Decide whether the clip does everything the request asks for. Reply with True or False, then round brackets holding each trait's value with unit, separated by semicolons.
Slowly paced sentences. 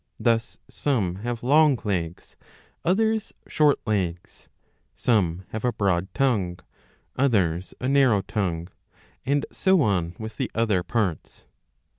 True (120 wpm)